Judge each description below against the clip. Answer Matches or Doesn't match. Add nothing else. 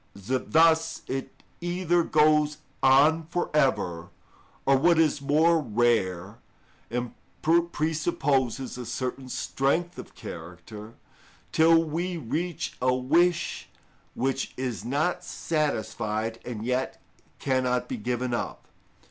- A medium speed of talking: Doesn't match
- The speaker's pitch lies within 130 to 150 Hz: Matches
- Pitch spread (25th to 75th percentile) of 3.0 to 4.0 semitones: Doesn't match